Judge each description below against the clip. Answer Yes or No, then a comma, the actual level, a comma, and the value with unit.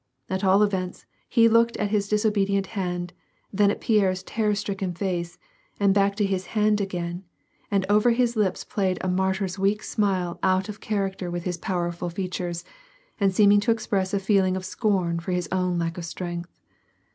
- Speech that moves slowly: No, average, 180 wpm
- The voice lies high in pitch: Yes, high, 195 Hz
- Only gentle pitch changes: Yes, narrow, 2.3 semitones